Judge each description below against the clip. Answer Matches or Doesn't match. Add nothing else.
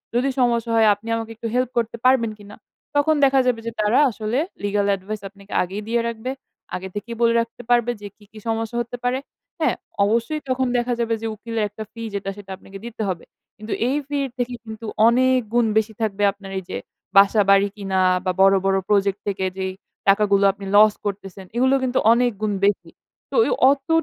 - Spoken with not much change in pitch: Doesn't match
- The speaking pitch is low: Doesn't match